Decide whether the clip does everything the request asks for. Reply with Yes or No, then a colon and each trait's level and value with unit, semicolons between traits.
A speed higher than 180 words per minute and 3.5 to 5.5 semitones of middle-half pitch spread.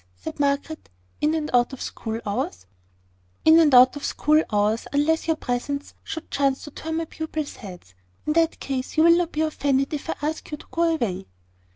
Yes: average, 200 wpm; average, 4.2 semitones